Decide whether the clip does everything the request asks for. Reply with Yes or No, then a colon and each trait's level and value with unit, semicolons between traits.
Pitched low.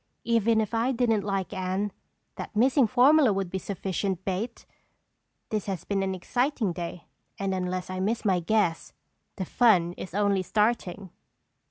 No: high, 200 Hz